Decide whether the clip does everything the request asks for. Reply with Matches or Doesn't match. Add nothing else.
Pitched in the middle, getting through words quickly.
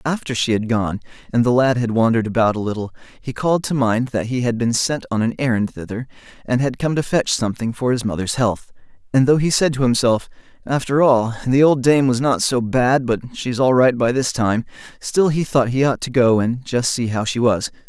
Doesn't match